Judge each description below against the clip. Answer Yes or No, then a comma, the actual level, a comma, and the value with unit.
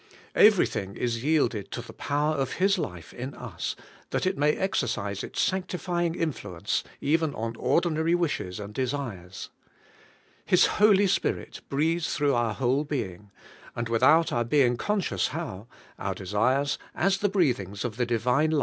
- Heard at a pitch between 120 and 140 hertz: Yes, low, 135 Hz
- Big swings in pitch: Yes, wide, 6.2 semitones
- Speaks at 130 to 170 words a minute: Yes, average, 150 wpm